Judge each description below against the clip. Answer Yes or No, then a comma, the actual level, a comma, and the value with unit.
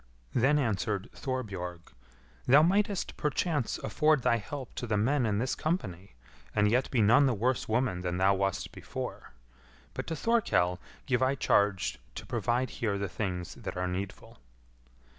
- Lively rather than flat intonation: Yes, wide, 5.7 semitones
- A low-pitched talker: Yes, low, 115 Hz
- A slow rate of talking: No, average, 160 wpm